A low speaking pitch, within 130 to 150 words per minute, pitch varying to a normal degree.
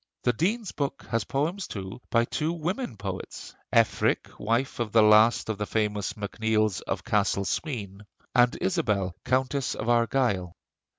Yes: low, 115 Hz; average, 145 wpm; average, 4.7 semitones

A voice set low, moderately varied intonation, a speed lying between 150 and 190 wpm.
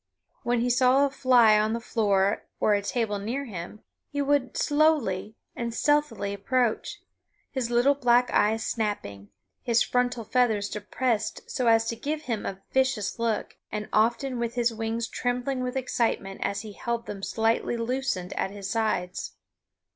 No: high, 230 Hz; average, 3.1 semitones; average, 155 wpm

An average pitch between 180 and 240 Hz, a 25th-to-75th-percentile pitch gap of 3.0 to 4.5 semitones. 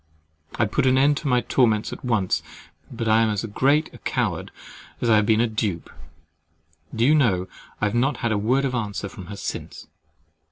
No: low, 115 Hz; average, 3.5 semitones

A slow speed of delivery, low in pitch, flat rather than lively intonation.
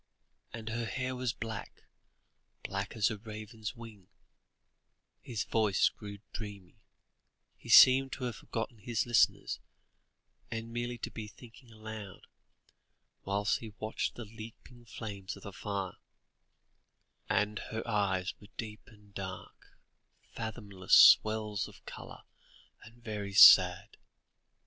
Yes: slow, 120 wpm; low, 110 Hz; narrow, 2.2 semitones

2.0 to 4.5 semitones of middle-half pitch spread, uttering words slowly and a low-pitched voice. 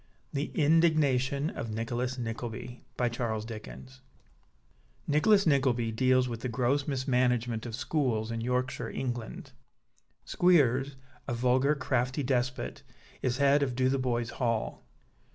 Yes: narrow, 2.6 semitones; slow, 105 wpm; low, 130 Hz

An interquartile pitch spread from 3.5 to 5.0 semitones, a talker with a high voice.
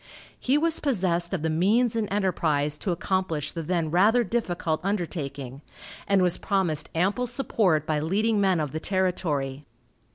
No: average, 4.7 semitones; medium, 180 Hz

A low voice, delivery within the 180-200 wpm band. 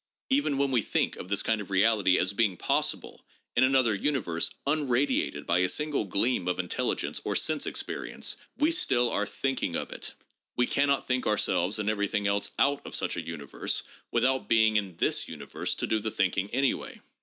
Yes: low, 110 Hz; average, 190 wpm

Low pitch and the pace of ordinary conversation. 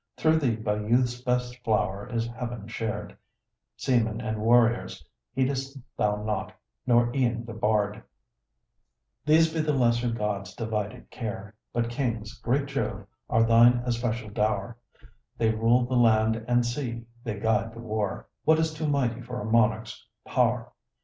Yes: low, 115 Hz; average, 150 wpm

